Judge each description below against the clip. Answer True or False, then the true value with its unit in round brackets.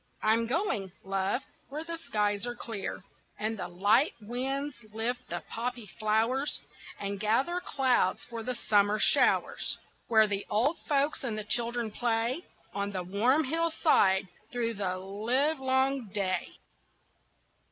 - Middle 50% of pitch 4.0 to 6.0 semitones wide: True (4.3 semitones)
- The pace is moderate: False (130 wpm)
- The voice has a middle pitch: False (230 Hz)